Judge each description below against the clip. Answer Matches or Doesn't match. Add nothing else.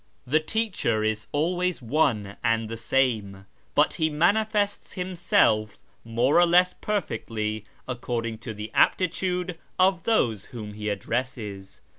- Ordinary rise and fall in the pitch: Doesn't match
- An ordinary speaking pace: Doesn't match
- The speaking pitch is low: Matches